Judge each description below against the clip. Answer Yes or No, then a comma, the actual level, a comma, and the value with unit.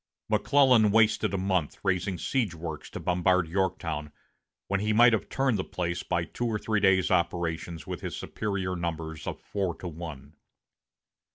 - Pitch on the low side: Yes, very low, 95 Hz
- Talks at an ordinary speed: Yes, average, 165 wpm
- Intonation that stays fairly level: No, average, 3.8 semitones